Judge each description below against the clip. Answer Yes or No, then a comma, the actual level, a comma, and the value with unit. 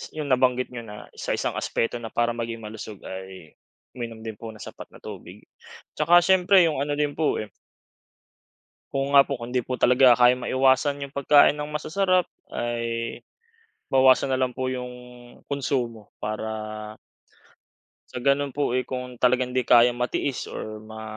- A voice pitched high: No, low, 125 Hz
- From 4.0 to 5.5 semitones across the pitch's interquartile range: No, average, 3.3 semitones